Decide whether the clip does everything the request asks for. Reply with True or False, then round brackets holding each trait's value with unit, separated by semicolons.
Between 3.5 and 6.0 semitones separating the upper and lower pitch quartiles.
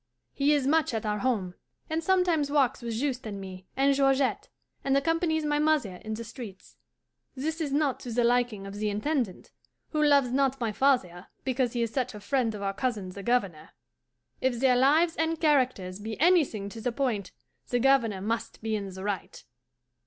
True (5.1 semitones)